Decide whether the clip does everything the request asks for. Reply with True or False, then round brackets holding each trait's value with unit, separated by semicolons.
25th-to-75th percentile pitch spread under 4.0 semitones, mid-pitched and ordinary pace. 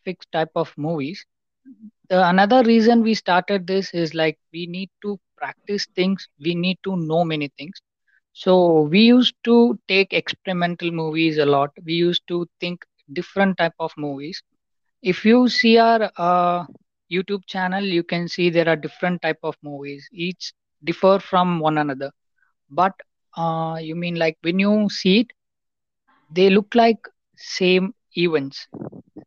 True (3.3 semitones; 180 Hz; 150 wpm)